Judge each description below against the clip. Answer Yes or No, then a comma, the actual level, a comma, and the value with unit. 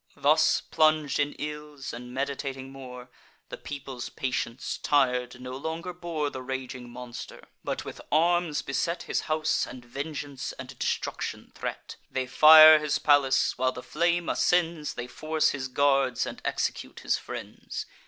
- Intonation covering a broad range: No, average, 3.3 semitones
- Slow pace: No, average, 145 wpm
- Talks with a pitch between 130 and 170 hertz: Yes, medium, 140 Hz